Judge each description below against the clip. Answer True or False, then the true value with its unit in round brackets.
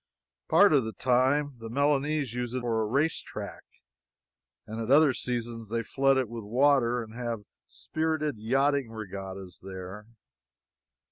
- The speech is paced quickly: False (145 wpm)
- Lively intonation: False (4.0 semitones)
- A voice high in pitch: False (120 Hz)